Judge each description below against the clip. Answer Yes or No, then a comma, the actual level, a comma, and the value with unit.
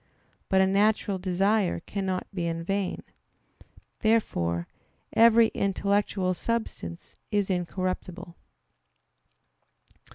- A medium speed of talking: No, slow, 85 wpm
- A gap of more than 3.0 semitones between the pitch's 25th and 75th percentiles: No, narrow, 2.4 semitones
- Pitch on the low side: No, high, 190 Hz